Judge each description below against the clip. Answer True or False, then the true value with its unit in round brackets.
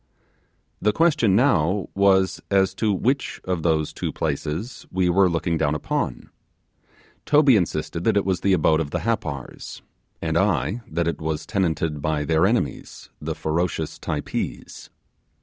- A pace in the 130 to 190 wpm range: True (150 wpm)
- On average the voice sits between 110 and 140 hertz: False (90 Hz)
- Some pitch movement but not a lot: True (4.2 semitones)